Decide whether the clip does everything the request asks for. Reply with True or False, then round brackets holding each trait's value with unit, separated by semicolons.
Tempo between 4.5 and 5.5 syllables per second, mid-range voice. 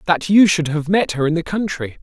True (5.4 syllables/s; 170 Hz)